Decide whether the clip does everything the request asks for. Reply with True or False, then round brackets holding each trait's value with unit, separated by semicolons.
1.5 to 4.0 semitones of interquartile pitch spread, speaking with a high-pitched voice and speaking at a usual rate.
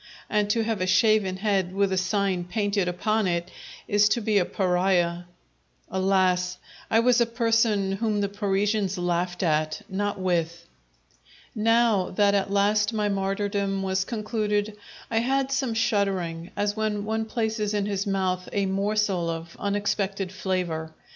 True (2.5 semitones; 200 Hz; 150 wpm)